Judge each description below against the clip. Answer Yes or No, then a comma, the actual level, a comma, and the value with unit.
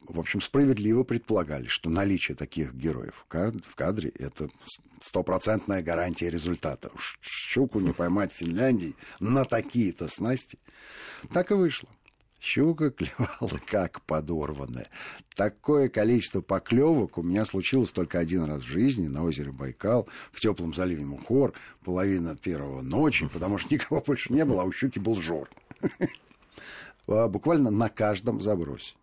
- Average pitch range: No, wide, 5.8 semitones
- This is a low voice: Yes, very low, 95 Hz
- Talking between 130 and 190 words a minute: Yes, average, 135 wpm